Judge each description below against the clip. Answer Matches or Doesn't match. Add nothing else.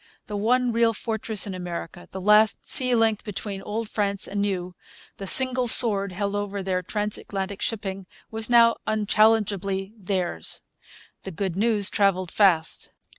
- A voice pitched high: Matches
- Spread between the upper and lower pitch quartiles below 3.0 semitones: Matches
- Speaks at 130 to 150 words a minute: Matches